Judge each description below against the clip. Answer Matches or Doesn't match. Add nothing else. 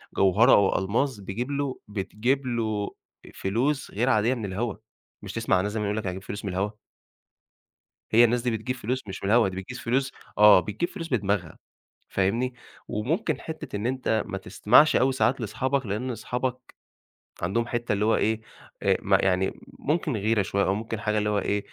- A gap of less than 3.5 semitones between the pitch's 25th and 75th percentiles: Doesn't match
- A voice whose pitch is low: Matches